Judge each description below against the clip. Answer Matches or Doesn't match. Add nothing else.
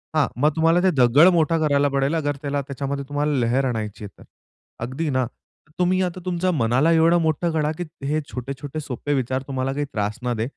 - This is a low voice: Doesn't match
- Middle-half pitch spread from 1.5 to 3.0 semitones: Doesn't match